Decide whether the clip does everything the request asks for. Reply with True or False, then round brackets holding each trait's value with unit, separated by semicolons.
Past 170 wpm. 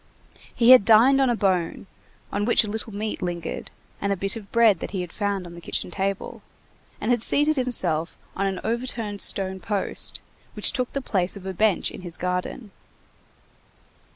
True (185 wpm)